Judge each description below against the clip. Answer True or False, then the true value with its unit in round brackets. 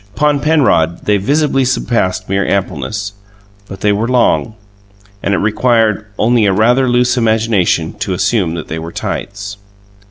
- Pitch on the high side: False (105 Hz)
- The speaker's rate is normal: True (150 wpm)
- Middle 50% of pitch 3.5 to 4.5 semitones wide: True (4.0 semitones)